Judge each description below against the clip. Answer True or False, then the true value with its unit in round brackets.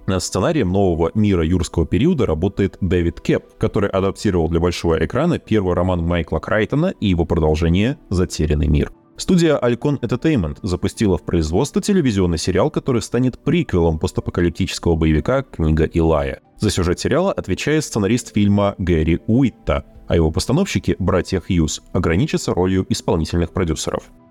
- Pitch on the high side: False (95 Hz)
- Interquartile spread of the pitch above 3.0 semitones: True (5.1 semitones)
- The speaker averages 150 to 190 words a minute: False (135 wpm)